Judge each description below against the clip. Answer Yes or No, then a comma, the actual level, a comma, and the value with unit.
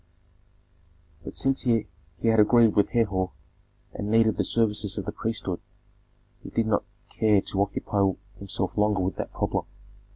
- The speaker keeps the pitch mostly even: Yes, narrow, 2.2 semitones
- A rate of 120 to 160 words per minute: Yes, average, 150 wpm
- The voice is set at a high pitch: No, low, 105 Hz